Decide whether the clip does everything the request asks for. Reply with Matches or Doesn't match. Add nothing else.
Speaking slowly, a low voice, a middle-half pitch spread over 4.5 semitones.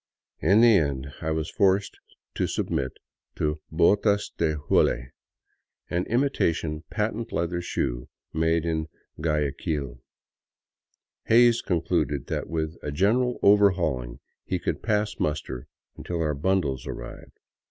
Matches